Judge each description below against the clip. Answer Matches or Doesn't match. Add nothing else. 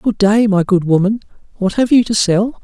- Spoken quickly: Matches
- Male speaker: Matches